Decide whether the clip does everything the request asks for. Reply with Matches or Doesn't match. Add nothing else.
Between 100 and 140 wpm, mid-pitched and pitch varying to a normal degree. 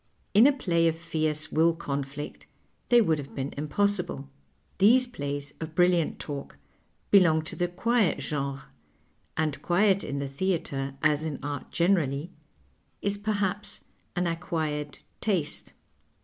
Matches